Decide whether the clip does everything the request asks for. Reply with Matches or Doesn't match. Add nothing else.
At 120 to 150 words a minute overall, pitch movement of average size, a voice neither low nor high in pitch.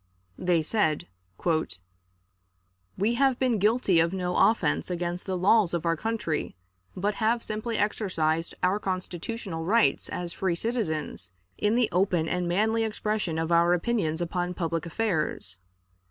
Matches